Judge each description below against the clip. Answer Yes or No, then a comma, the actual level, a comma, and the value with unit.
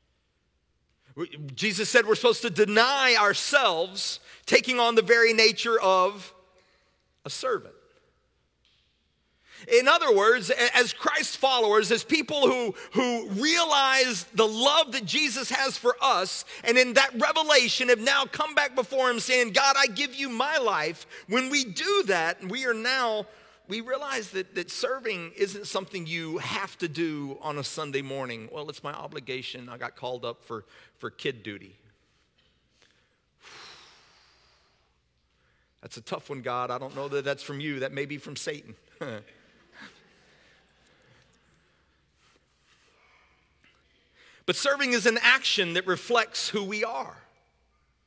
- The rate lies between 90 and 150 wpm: Yes, average, 140 wpm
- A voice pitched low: No, high, 220 Hz